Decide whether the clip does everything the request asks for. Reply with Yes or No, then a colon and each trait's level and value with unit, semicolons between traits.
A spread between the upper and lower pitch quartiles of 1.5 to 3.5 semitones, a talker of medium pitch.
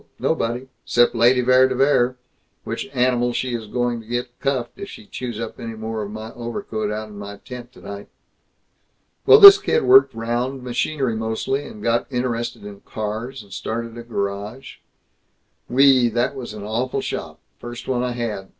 No: narrow, 2.5 semitones; low, 120 Hz